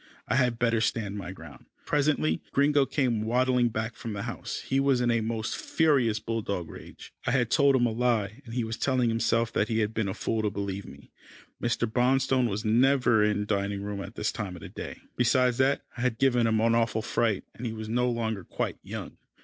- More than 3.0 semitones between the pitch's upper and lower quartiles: No, average, 2.7 semitones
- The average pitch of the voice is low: Yes, low, 115 Hz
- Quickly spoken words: Yes, fast, 220 wpm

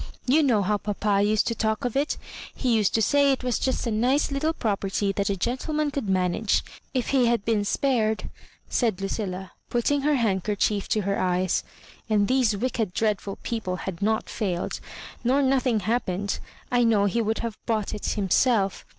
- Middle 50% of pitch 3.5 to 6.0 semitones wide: Yes, average, 3.8 semitones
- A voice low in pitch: No, high, 220 Hz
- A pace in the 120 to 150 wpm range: No, average, 185 wpm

